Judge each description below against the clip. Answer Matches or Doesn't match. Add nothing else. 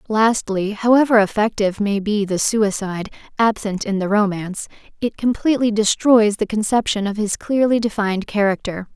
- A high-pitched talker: Matches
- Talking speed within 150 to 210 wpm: Doesn't match